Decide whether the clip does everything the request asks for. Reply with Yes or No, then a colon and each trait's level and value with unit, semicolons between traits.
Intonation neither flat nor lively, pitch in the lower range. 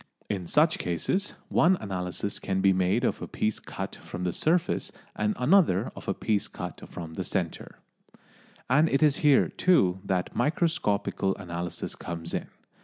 No: wide, 8.9 semitones; low, 100 Hz